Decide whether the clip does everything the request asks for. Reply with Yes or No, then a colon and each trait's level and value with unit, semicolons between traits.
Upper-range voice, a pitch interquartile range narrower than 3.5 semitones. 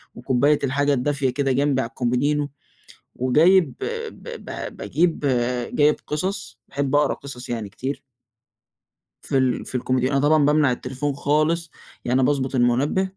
No: medium, 140 Hz; narrow, 2.5 semitones